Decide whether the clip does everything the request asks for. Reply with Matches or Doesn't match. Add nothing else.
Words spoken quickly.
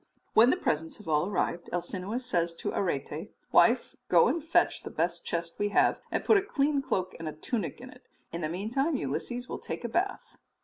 Matches